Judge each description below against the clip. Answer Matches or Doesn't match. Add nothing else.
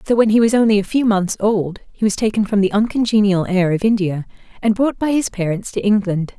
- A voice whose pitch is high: Matches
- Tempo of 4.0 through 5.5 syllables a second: Doesn't match